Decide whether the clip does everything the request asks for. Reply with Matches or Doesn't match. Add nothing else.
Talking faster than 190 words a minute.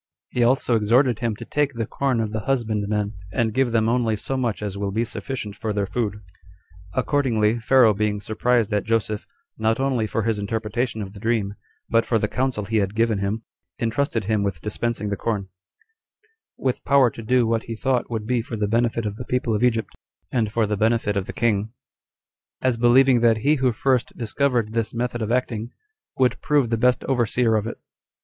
Matches